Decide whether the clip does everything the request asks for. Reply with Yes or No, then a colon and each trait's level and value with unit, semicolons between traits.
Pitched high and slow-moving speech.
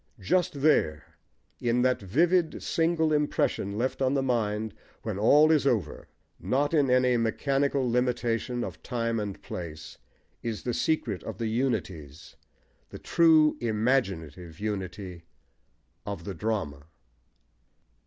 No: low, 115 Hz; slow, 125 wpm